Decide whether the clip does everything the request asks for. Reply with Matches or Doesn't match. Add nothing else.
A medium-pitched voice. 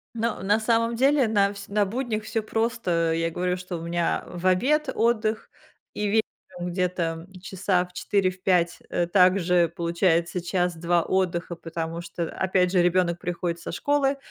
Matches